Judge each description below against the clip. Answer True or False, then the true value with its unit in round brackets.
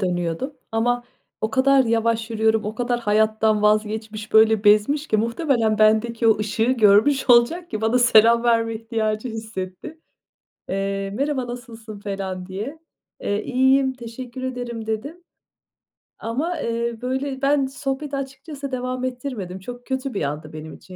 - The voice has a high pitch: True (230 Hz)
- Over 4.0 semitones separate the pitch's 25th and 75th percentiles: False (3.4 semitones)